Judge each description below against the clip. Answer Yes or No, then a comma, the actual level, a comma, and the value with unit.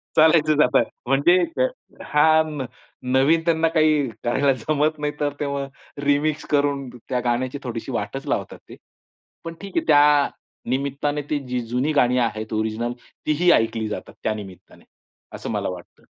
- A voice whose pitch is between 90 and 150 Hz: Yes, medium, 140 Hz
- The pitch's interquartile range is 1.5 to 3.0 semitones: No, average, 3.6 semitones